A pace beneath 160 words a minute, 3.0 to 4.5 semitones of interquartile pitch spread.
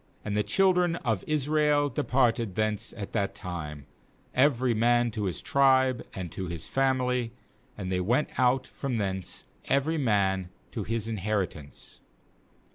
No: average, 145 wpm; average, 5.3 semitones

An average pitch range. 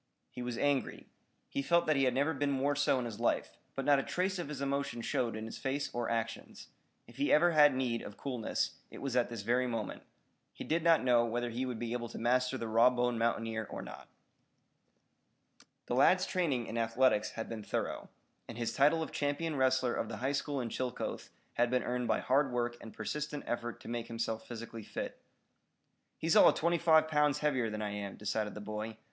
Yes: average, 3.7 semitones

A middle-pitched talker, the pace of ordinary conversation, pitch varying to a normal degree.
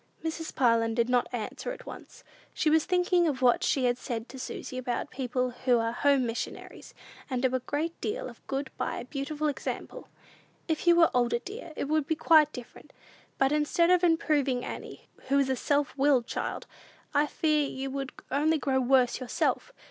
No: very high, 275 Hz; average, 190 wpm; average, 3.7 semitones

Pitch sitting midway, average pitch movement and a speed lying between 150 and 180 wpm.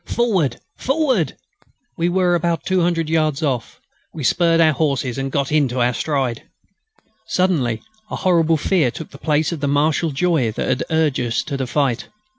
Yes: medium, 155 Hz; average, 4.0 semitones; average, 170 wpm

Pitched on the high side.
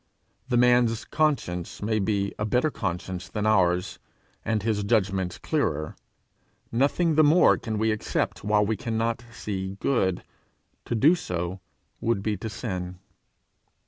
No: low, 105 Hz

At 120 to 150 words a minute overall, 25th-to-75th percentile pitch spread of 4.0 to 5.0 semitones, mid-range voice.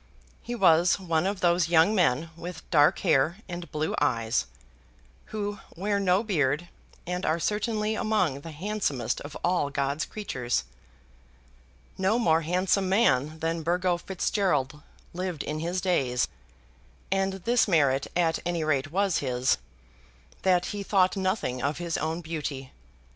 Yes: average, 140 wpm; average, 4.3 semitones; medium, 170 Hz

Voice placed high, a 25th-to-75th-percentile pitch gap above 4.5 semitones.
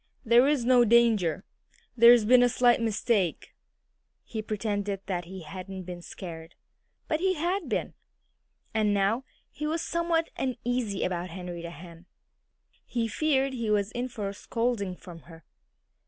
Yes: high, 220 Hz; average, 5.2 semitones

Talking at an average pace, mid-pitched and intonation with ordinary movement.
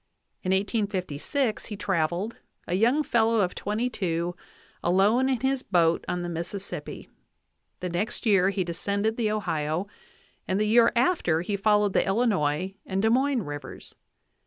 No: average, 150 wpm; high, 200 Hz; average, 4.3 semitones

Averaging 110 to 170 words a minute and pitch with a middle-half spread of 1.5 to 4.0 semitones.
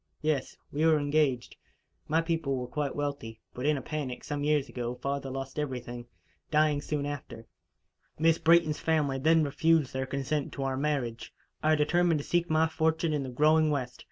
No: average, 180 wpm; average, 2.8 semitones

